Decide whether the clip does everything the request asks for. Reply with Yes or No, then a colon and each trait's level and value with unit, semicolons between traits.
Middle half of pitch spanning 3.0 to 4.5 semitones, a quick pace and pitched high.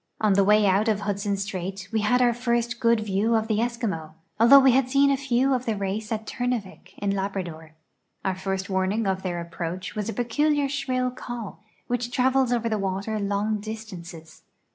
No: average, 3.8 semitones; average, 195 wpm; high, 215 Hz